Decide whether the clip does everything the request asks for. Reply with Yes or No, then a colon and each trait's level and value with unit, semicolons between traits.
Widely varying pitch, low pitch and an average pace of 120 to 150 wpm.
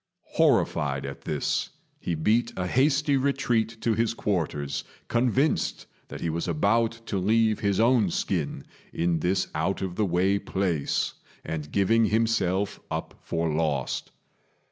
Yes: wide, 5.7 semitones; very low, 95 Hz; average, 140 wpm